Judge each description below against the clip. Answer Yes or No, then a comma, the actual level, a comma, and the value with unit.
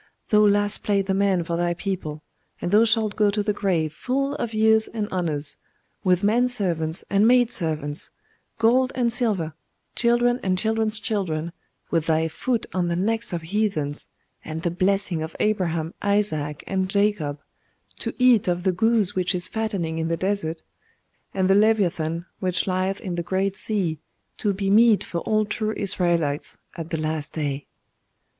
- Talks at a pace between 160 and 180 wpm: Yes, average, 170 wpm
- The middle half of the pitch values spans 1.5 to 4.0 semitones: No, average, 4.4 semitones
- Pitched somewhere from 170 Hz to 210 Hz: Yes, high, 190 Hz